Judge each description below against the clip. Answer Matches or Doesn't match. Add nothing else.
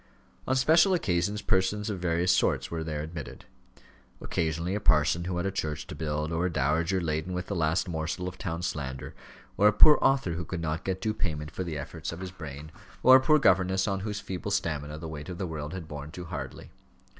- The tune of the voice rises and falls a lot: Doesn't match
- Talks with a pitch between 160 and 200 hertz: Doesn't match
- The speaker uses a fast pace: Matches